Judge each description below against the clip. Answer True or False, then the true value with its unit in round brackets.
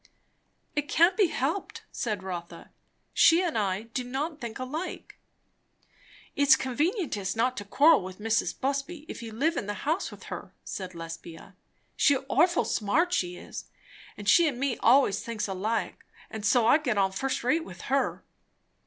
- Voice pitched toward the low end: False (250 Hz)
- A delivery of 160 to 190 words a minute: True (170 wpm)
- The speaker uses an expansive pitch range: True (6.8 semitones)